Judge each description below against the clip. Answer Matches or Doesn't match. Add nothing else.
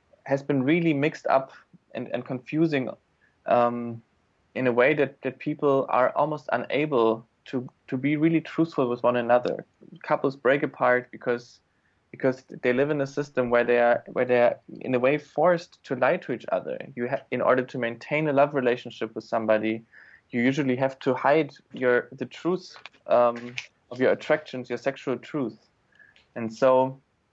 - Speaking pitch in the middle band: Doesn't match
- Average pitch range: Matches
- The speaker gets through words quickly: Doesn't match